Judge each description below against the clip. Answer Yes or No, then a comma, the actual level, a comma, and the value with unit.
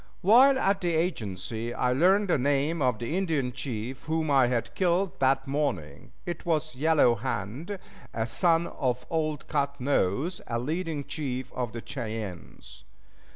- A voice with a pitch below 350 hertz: Yes, medium, 140 Hz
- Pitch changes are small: No, wide, 5.4 semitones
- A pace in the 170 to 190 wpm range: No, average, 155 wpm